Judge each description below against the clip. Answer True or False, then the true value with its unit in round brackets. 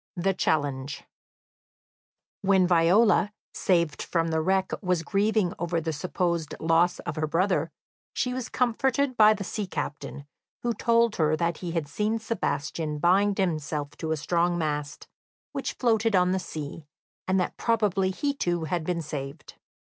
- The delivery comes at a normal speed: True (155 wpm)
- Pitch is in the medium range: True (175 Hz)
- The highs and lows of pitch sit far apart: False (4.5 semitones)